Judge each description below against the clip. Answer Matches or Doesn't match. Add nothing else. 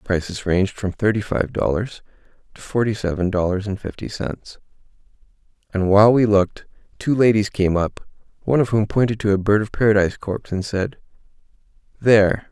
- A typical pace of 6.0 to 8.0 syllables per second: Doesn't match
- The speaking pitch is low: Matches